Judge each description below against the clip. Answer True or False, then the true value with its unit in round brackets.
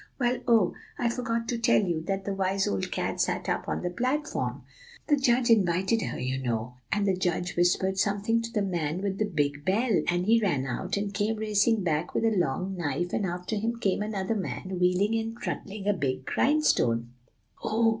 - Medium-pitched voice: False (195 Hz)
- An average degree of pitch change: True (4.3 semitones)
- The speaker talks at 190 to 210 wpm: True (200 wpm)